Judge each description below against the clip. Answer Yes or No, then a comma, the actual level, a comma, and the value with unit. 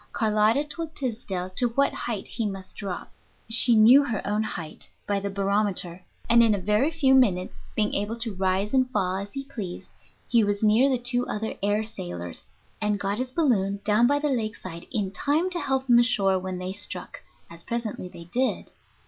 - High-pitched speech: Yes, high, 215 Hz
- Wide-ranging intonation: No, average, 4.2 semitones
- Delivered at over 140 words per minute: Yes, average, 195 wpm